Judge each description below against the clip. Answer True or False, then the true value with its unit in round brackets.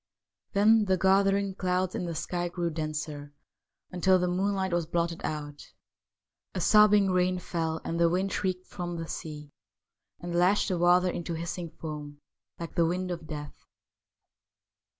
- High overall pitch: False (175 Hz)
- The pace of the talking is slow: False (155 wpm)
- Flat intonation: True (2.2 semitones)